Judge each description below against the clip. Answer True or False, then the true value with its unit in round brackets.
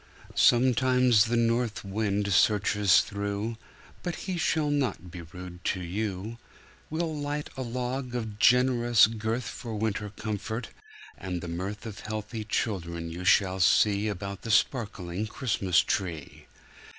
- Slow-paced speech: True (130 wpm)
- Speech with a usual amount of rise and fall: True (3.8 semitones)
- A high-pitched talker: False (110 Hz)